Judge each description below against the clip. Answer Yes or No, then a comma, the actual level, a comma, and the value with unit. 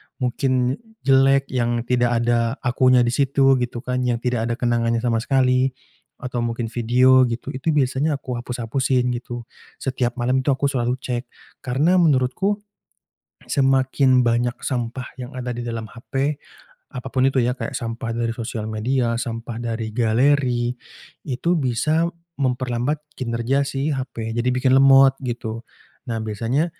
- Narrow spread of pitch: Yes, narrow, 2.0 semitones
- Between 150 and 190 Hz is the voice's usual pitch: No, low, 125 Hz